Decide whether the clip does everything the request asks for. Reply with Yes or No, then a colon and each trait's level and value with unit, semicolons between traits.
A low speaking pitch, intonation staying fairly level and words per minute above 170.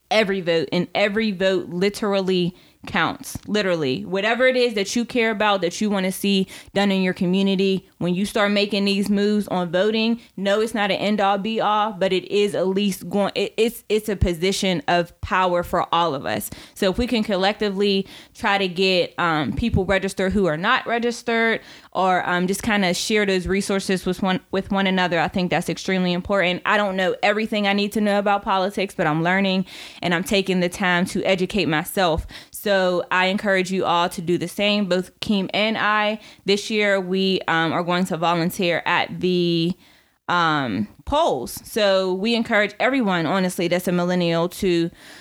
No: high, 195 Hz; narrow, 2.2 semitones; average, 190 wpm